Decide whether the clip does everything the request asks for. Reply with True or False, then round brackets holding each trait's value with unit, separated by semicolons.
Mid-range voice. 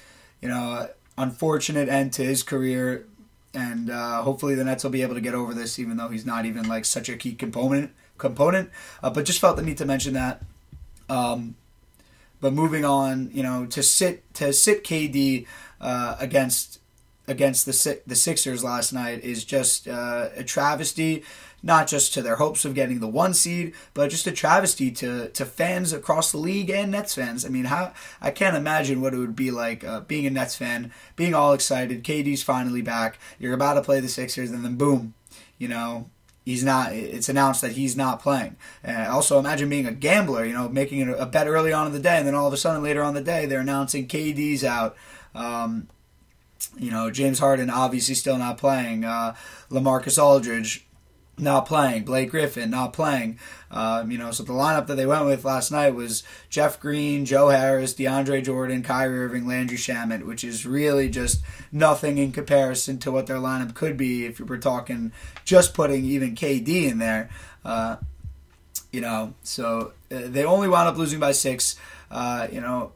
False (130 Hz)